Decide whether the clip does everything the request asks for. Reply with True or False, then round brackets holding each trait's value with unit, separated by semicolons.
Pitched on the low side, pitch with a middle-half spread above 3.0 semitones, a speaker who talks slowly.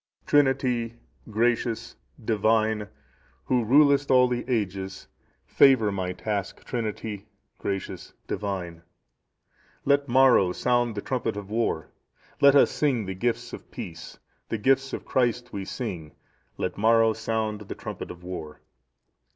True (110 Hz; 3.8 semitones; 125 wpm)